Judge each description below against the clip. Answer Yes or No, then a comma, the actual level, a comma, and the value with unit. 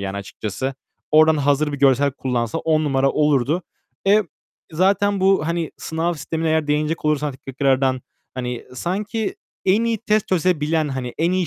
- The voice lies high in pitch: No, medium, 155 Hz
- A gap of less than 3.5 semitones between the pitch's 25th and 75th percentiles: No, average, 4.7 semitones